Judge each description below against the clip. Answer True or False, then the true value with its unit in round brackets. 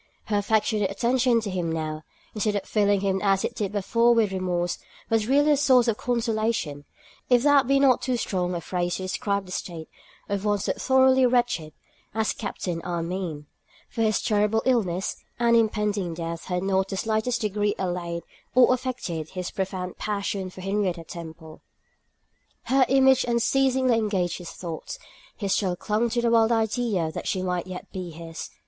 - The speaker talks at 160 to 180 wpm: True (175 wpm)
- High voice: True (205 Hz)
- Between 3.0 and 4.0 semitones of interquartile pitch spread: False (4.6 semitones)